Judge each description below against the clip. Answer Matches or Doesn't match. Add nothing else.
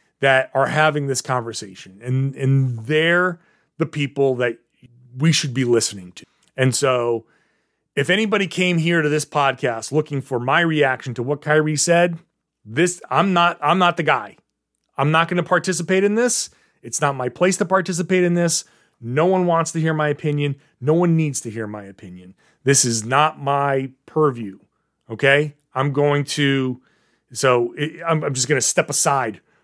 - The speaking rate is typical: Matches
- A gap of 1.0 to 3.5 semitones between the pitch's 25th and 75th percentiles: Doesn't match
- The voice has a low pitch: Doesn't match